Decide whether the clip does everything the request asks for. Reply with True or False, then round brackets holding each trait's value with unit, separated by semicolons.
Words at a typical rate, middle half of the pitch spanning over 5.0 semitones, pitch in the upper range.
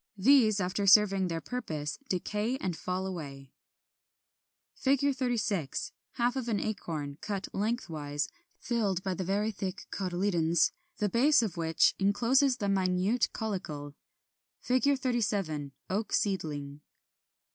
False (120 wpm; 5.5 semitones; 195 Hz)